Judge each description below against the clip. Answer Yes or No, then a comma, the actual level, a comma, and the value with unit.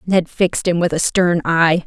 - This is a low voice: No, medium, 170 Hz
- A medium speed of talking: No, fast, 225 wpm